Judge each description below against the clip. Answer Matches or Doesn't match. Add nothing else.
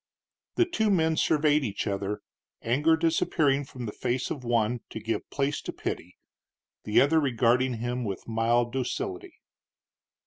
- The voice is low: Matches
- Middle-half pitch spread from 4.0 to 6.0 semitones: Matches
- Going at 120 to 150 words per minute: Matches